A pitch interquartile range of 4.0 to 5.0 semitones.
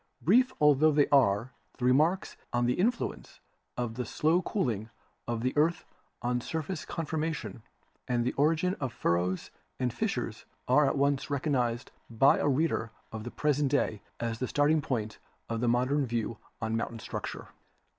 Yes: average, 4.3 semitones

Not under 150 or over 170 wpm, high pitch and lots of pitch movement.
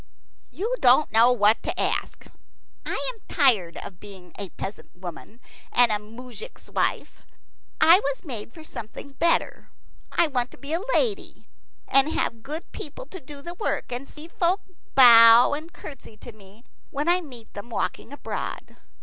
Yes: average, 165 wpm; very high, 260 Hz; wide, 6.2 semitones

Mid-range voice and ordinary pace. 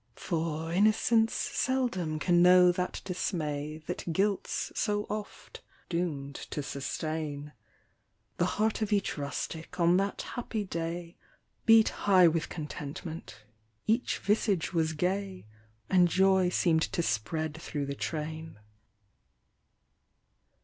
No: medium, 175 Hz; slow, 115 wpm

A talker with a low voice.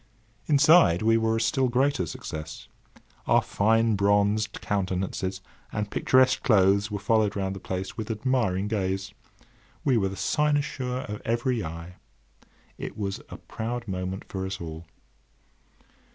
Yes: low, 105 Hz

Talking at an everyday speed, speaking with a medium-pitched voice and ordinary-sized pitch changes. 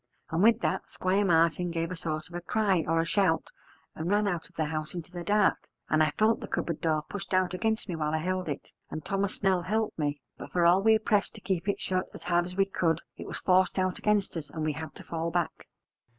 No: fast, 250 wpm; medium, 175 Hz; average, 3.2 semitones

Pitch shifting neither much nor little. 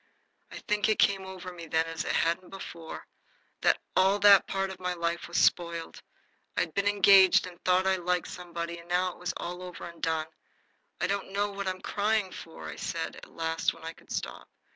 No: narrow, 2.3 semitones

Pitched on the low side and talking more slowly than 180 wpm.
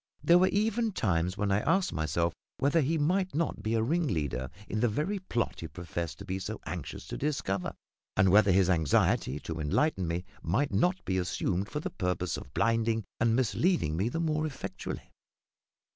No: low, 110 Hz; average, 185 wpm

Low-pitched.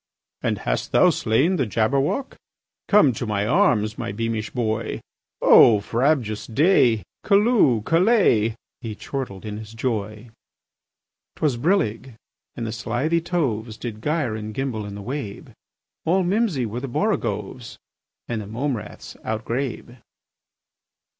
Yes: low, 120 Hz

